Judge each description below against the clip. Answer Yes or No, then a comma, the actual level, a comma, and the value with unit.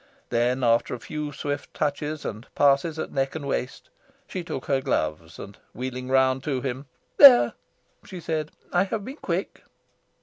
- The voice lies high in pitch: No, low, 135 Hz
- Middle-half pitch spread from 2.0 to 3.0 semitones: No, average, 3.4 semitones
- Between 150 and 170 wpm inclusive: Yes, average, 165 wpm